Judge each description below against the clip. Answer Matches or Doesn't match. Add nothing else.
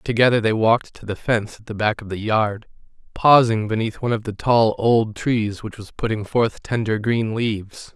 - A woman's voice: Doesn't match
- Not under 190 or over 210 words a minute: Matches